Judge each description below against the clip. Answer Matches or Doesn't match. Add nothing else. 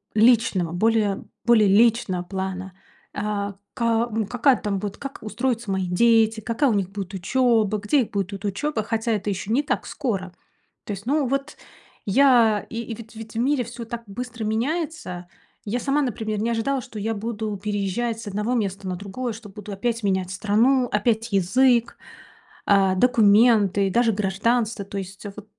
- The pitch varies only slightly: Doesn't match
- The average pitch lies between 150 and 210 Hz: Doesn't match